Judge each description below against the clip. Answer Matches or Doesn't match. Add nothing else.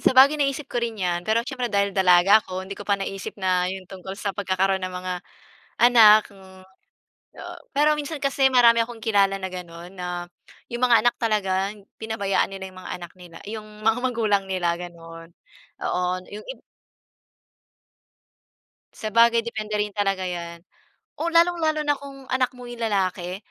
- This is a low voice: Doesn't match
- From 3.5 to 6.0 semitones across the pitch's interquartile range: Matches